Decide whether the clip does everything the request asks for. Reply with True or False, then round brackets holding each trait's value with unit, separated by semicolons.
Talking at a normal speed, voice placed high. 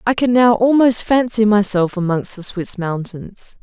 True (165 wpm; 210 Hz)